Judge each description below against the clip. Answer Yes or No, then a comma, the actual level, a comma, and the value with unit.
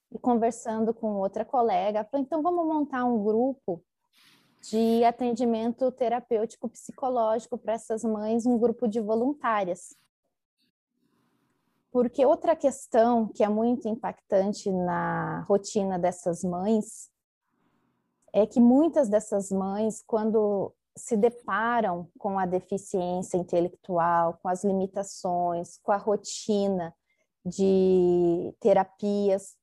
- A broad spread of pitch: No, average, 3.8 semitones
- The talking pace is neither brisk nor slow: No, slow, 105 wpm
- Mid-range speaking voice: No, high, 215 Hz